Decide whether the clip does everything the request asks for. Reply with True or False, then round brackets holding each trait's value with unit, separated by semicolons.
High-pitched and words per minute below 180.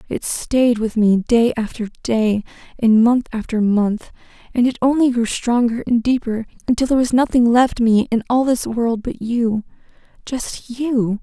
True (235 Hz; 165 wpm)